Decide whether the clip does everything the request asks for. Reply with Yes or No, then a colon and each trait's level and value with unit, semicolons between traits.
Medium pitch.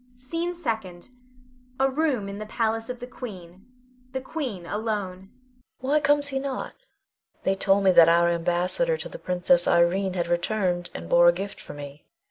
No: high, 200 Hz